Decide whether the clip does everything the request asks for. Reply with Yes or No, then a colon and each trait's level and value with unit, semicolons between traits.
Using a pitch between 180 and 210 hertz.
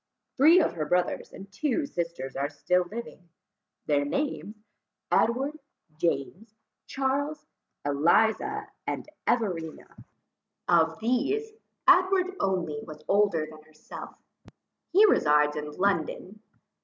Yes: high, 190 Hz